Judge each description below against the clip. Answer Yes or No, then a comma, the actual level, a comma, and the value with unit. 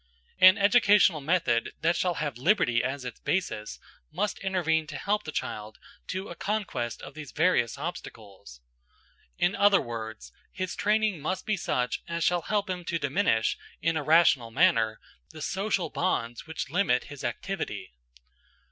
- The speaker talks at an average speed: Yes, average, 155 wpm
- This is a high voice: No, medium, 165 Hz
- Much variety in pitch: Yes, wide, 7.2 semitones